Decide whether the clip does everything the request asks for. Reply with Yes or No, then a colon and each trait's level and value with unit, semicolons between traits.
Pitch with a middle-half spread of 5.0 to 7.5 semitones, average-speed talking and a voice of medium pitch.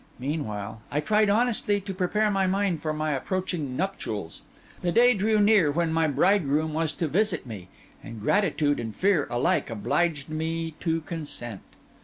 Yes: average, 5.3 semitones; average, 160 wpm; medium, 165 Hz